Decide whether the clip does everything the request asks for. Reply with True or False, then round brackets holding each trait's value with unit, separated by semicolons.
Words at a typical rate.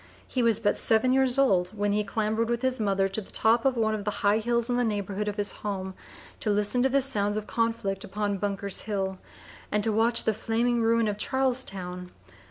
False (215 wpm)